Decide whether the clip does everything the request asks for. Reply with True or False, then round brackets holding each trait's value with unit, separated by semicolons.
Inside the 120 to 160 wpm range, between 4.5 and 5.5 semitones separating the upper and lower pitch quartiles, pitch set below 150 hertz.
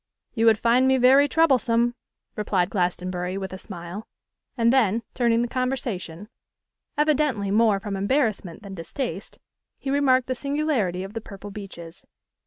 False (145 wpm; 5.0 semitones; 225 Hz)